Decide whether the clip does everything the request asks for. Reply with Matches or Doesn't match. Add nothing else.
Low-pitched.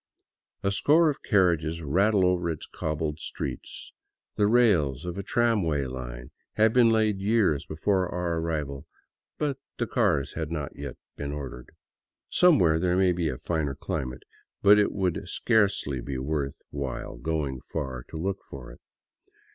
Matches